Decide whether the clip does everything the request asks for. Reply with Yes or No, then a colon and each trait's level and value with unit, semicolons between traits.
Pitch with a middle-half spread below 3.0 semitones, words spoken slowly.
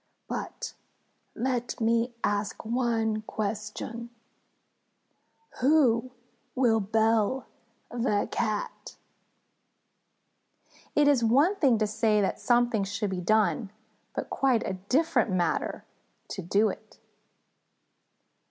Yes: narrow, 2.6 semitones; slow, 95 wpm